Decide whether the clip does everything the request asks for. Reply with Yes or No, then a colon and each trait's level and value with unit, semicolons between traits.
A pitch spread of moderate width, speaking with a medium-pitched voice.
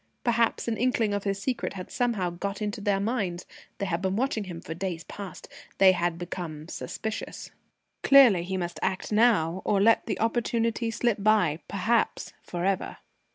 No: average, 4.2 semitones; high, 200 Hz